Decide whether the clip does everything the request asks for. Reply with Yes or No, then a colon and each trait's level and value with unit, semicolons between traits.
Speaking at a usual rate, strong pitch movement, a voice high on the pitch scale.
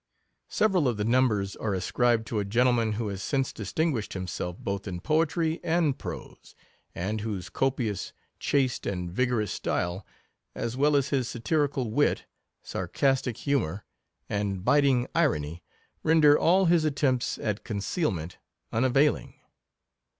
No: average, 145 wpm; wide, 5.9 semitones; low, 120 Hz